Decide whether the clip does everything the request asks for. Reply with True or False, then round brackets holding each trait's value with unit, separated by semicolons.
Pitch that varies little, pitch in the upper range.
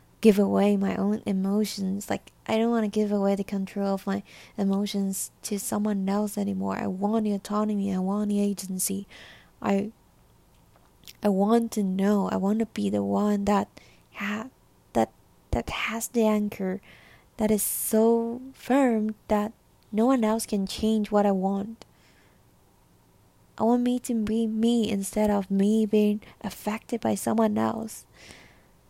True (1.8 semitones; 205 Hz)